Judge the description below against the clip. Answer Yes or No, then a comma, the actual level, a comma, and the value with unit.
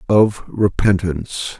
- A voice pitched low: Yes, very low, 95 Hz